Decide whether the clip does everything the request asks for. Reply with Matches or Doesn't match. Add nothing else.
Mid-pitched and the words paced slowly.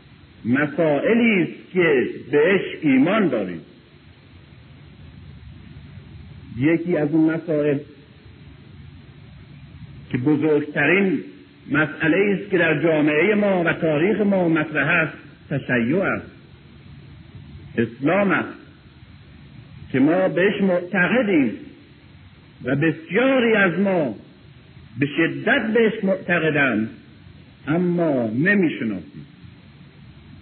Matches